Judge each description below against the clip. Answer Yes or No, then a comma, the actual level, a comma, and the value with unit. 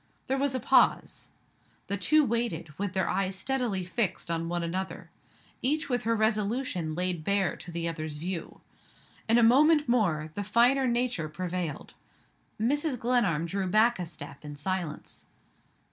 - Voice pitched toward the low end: No, high, 195 Hz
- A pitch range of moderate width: No, wide, 6.2 semitones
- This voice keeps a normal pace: Yes, average, 155 wpm